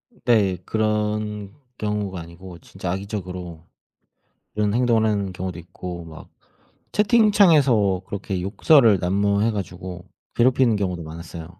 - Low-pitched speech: Yes, low, 100 Hz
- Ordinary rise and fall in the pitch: Yes, average, 3.2 semitones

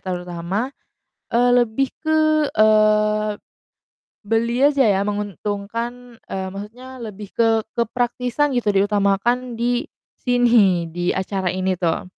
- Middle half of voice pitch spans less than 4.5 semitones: Yes, average, 3.7 semitones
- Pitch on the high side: Yes, high, 215 Hz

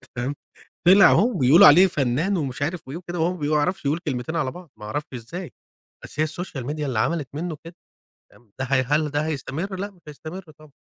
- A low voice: No, medium, 155 Hz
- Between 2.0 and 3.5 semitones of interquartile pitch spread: No, average, 4.2 semitones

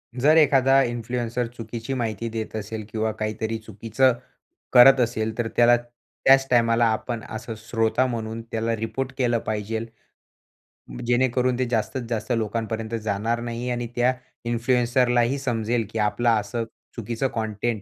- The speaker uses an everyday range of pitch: No, narrow, 1.7 semitones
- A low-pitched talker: Yes, low, 115 Hz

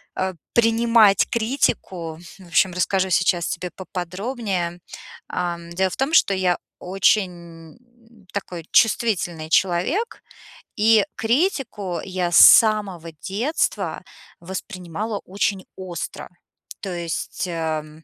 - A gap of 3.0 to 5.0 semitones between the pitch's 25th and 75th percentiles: Yes, average, 3.9 semitones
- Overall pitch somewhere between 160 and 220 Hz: Yes, medium, 185 Hz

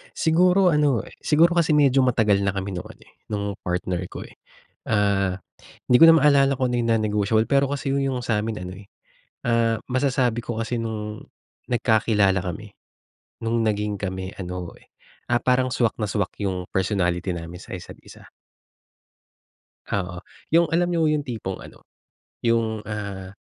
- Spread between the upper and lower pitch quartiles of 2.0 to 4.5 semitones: No, average, 4.9 semitones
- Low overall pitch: Yes, low, 110 Hz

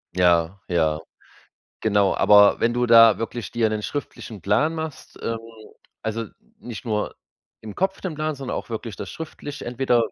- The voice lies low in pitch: Yes, low, 115 Hz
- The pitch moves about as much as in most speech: Yes, average, 4.6 semitones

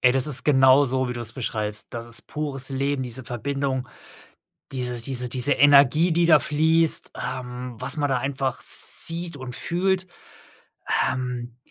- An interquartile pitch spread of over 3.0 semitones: No, average, 2.7 semitones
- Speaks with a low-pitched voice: Yes, low, 130 Hz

